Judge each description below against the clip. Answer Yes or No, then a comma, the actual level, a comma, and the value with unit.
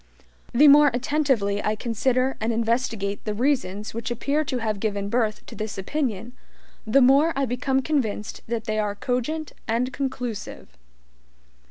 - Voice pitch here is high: Yes, high, 240 Hz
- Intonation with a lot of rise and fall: No, average, 3.9 semitones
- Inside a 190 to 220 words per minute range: No, average, 150 wpm